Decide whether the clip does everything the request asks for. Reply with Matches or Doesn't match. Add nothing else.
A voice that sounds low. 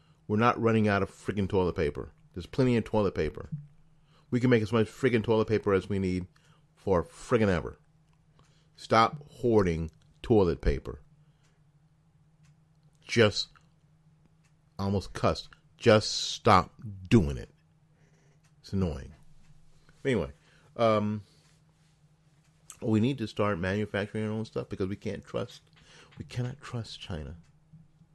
Matches